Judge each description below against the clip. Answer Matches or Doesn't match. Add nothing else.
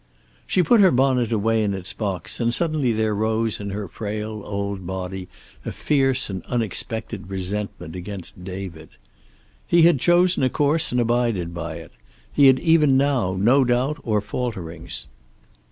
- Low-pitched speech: Matches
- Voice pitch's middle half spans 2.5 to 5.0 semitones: Doesn't match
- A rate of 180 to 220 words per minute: Doesn't match